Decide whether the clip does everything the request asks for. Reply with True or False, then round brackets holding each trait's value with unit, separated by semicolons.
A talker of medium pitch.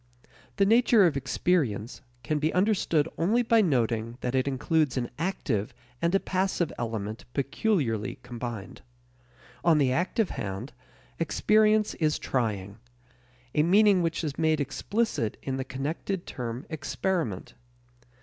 True (150 Hz)